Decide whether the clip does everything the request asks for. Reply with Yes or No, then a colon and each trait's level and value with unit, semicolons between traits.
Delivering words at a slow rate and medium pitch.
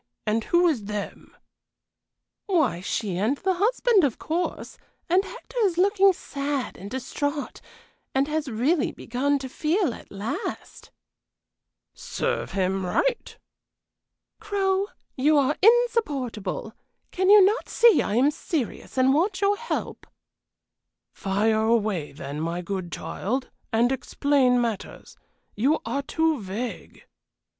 No: slow, 125 wpm; very high, 275 Hz